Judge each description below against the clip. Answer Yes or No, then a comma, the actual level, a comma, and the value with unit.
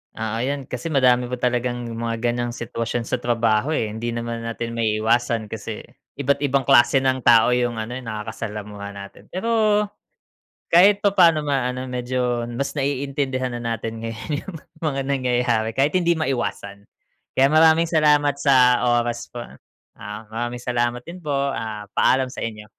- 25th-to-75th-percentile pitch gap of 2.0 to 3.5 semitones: Yes, average, 3.2 semitones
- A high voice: No, low, 125 Hz